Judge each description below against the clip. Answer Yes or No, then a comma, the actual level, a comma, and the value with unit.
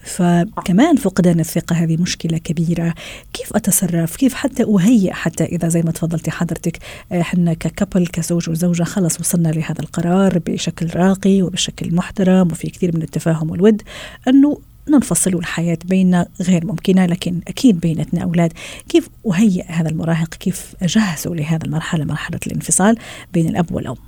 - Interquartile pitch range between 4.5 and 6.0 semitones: No, narrow, 2.4 semitones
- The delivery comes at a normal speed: No, fast, 140 wpm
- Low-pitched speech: No, medium, 175 Hz